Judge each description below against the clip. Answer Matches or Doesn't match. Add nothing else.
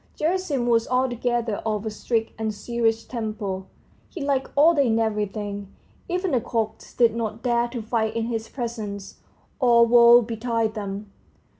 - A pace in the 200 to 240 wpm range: Doesn't match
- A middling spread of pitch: Doesn't match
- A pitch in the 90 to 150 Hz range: Doesn't match